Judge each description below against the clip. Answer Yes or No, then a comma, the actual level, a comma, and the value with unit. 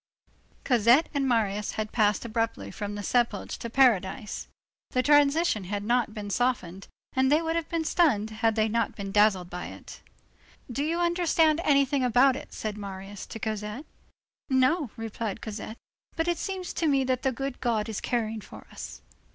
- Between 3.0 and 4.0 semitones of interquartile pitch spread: No, average, 4.9 semitones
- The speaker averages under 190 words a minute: Yes, average, 175 wpm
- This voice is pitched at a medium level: No, high, 235 Hz